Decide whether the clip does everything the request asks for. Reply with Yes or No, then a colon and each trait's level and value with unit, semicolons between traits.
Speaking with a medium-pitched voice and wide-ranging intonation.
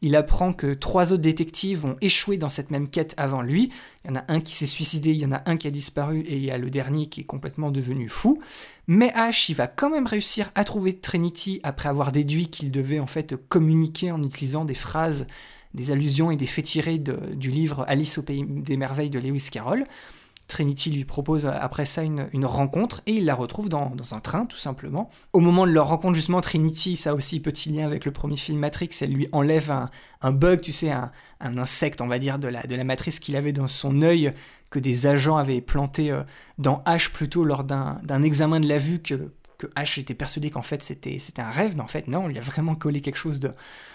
No: medium, 150 Hz; average, 3.0 semitones